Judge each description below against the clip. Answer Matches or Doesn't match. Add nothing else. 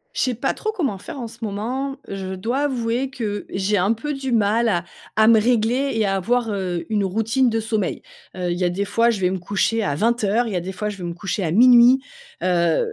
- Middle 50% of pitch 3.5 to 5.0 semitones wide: Matches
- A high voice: Matches